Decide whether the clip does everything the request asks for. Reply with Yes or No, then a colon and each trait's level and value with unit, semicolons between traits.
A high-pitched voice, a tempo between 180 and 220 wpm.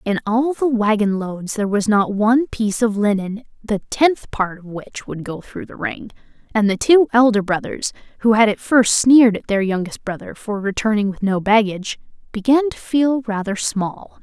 Yes: high, 220 Hz; average, 195 wpm